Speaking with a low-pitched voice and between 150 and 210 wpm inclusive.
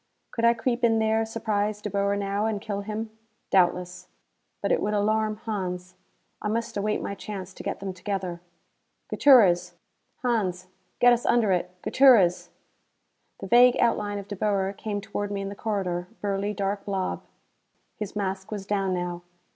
No: high, 205 Hz; average, 165 wpm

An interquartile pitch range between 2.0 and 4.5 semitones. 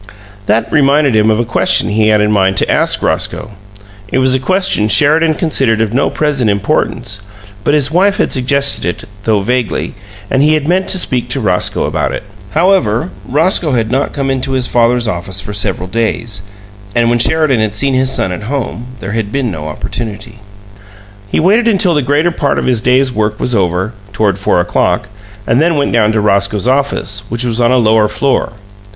No: average, 4.9 semitones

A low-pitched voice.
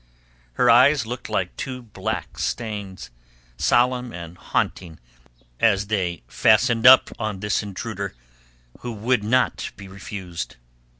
Yes: low, 110 Hz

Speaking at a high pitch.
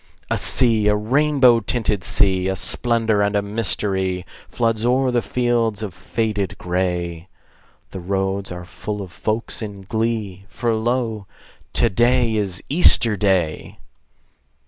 No: low, 105 Hz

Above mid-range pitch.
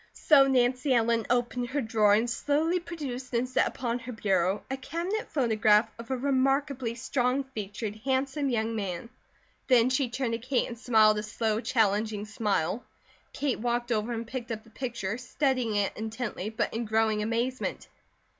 Yes: high, 235 Hz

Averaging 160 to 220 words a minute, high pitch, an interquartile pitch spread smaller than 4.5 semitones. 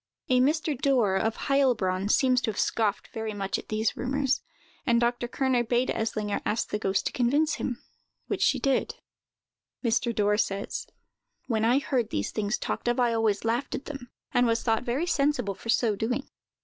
Yes: average, 185 wpm; high, 235 Hz; average, 3.2 semitones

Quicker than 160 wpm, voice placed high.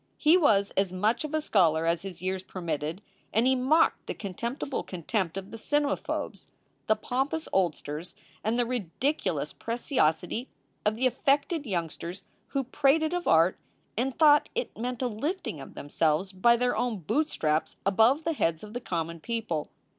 Yes: average, 170 wpm; high, 220 Hz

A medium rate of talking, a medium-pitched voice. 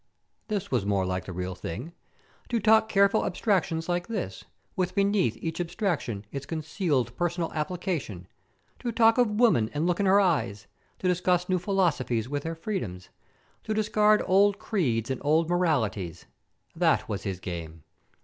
Yes: average, 160 wpm; medium, 170 Hz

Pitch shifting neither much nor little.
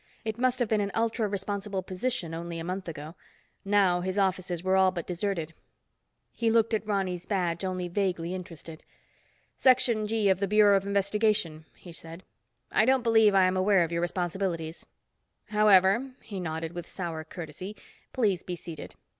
Yes: average, 3.4 semitones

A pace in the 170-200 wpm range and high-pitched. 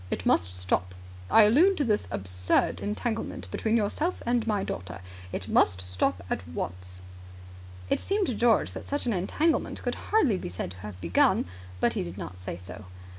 No: average, 180 wpm; low, 105 Hz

